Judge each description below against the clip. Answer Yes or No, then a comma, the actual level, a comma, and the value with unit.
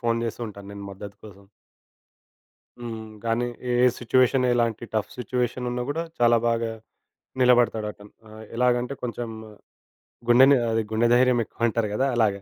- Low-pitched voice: Yes, low, 120 Hz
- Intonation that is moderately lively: No, narrow, 2.0 semitones